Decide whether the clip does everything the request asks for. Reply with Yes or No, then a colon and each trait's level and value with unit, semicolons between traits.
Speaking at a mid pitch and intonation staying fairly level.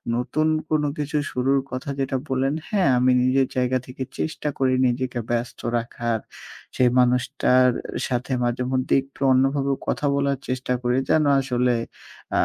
No: low, 130 Hz; narrow, 1.6 semitones